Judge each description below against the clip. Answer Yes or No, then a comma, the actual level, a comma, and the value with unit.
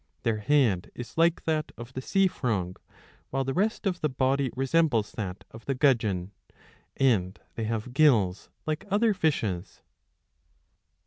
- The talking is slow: No, average, 150 wpm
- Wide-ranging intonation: Yes, wide, 6.2 semitones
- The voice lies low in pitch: Yes, low, 130 Hz